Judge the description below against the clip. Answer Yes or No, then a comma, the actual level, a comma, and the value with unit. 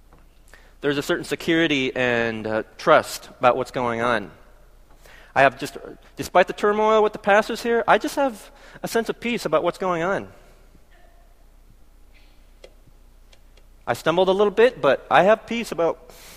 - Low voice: No, medium, 150 Hz